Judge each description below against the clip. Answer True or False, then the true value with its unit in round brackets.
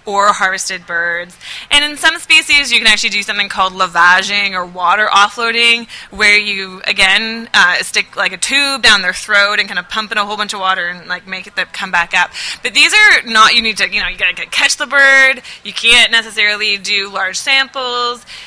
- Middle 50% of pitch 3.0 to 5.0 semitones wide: True (4.2 semitones)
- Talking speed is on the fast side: True (215 wpm)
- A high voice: True (210 Hz)